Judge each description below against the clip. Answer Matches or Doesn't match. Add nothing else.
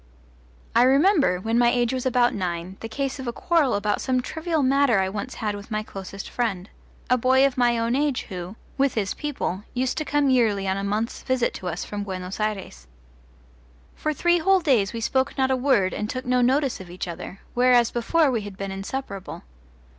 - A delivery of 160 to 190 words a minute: Doesn't match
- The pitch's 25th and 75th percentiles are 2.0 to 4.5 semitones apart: Doesn't match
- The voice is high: Matches